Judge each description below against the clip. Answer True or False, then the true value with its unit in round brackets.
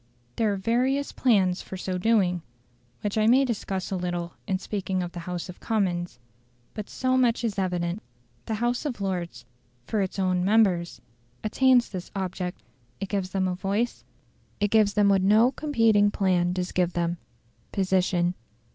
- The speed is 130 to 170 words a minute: True (165 wpm)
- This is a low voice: False (195 Hz)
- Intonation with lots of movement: False (3.5 semitones)